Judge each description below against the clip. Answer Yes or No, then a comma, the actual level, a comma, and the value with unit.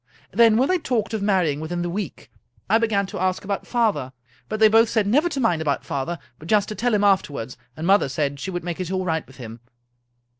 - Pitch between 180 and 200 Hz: Yes, high, 190 Hz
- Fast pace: Yes, fast, 240 wpm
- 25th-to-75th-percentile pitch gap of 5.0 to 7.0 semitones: Yes, wide, 5.5 semitones